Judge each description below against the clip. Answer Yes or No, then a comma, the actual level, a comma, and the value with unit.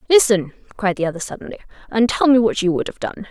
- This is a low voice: No, high, 215 Hz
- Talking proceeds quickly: Yes, fast, 235 wpm